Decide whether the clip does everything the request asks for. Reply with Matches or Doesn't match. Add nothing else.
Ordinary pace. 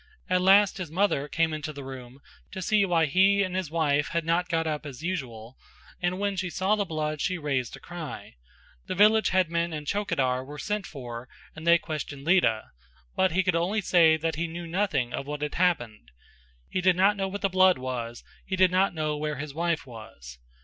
Doesn't match